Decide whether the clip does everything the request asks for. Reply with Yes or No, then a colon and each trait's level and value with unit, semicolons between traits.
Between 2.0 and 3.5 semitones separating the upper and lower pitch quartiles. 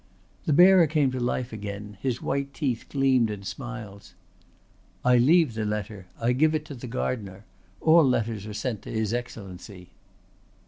No: average, 4.5 semitones